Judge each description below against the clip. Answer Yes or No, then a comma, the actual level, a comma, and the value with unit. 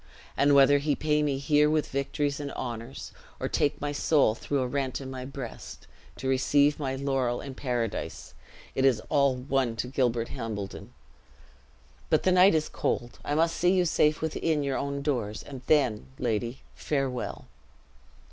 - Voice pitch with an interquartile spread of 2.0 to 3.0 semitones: Yes, average, 2.7 semitones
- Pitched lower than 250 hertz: Yes, medium, 140 Hz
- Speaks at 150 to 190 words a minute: Yes, average, 165 wpm